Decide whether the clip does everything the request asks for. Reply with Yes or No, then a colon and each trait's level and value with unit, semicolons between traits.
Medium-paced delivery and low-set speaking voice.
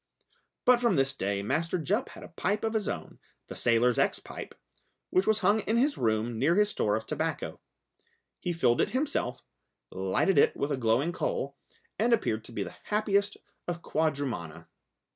No: average, 180 wpm; medium, 165 Hz